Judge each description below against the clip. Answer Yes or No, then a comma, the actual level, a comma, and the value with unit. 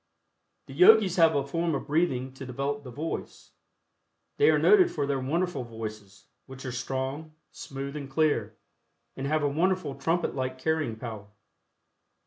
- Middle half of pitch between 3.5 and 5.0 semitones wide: Yes, average, 3.8 semitones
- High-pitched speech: No, medium, 140 Hz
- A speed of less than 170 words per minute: Yes, average, 155 wpm